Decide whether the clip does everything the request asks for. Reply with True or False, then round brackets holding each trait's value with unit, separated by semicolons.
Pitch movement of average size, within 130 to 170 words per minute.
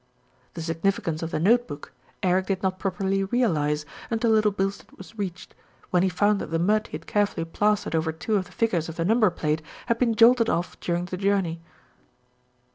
False (4.1 semitones; 200 wpm)